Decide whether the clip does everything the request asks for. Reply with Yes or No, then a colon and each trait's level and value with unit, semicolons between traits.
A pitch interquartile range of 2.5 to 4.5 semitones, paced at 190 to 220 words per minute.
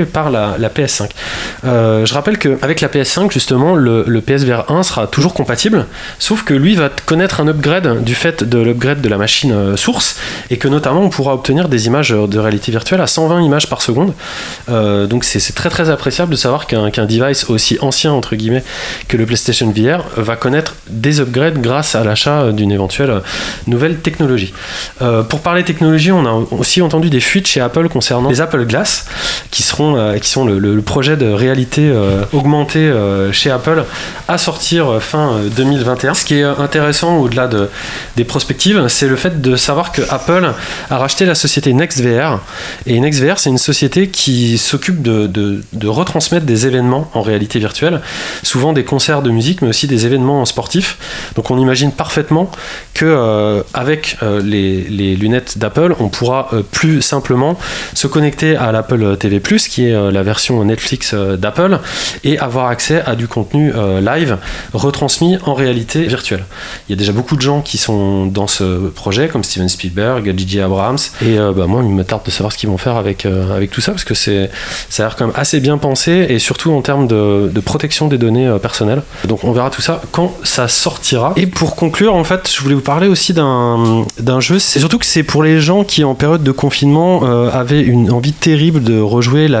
No: wide, 5.6 semitones; average, 195 wpm